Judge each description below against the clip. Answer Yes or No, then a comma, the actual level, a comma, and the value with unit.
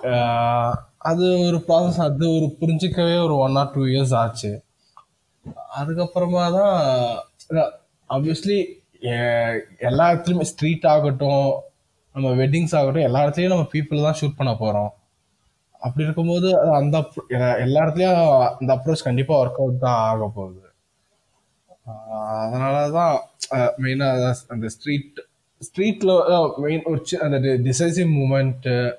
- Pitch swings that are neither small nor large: Yes, average, 4.8 semitones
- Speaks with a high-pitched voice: No, medium, 145 Hz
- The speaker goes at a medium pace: Yes, average, 110 wpm